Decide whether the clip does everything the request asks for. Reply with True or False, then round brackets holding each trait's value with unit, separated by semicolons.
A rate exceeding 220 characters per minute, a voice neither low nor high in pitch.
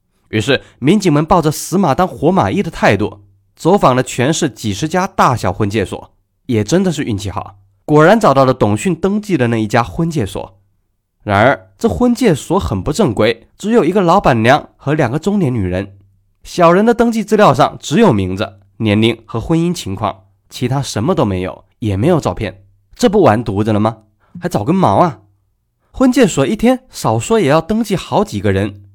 False (280 characters per minute; 120 Hz)